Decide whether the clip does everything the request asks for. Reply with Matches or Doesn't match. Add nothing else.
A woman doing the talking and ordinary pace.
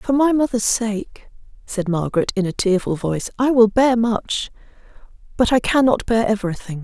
Matches